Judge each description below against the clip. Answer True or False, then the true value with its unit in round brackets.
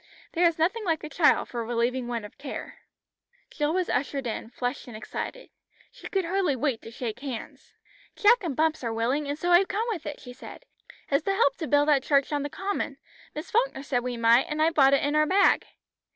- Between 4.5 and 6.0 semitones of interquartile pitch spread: True (5.4 semitones)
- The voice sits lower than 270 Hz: False (290 Hz)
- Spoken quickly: True (225 wpm)